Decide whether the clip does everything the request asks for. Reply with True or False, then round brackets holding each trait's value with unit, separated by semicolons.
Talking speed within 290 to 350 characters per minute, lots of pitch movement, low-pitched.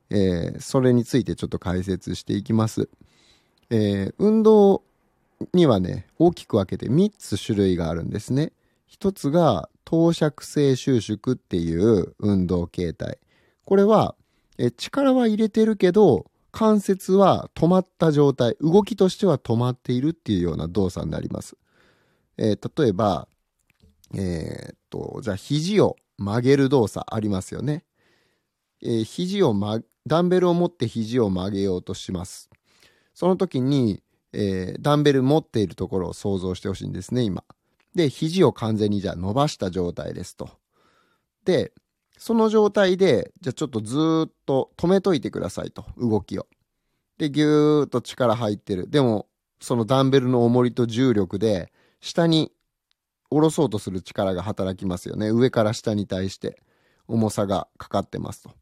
True (300 characters per minute; 7.9 semitones; 120 Hz)